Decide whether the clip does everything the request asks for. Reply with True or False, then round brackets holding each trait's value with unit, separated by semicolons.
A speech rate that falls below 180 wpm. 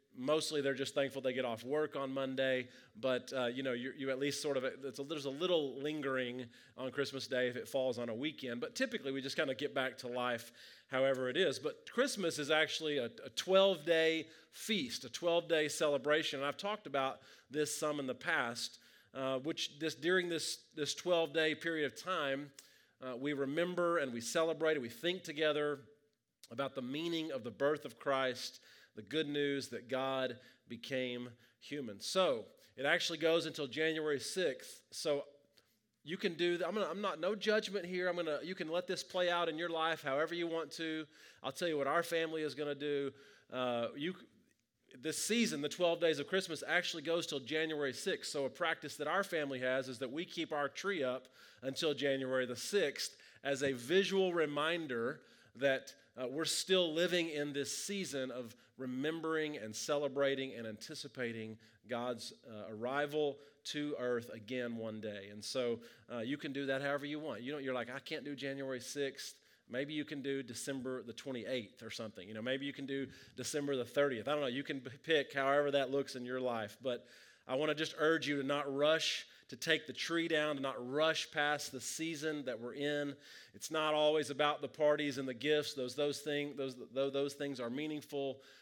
False (200 wpm)